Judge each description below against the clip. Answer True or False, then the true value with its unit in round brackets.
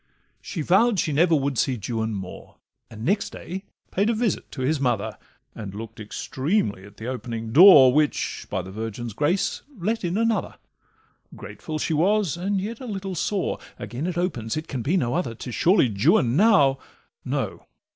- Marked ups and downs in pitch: True (8.5 semitones)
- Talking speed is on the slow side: False (175 wpm)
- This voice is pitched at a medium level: True (145 Hz)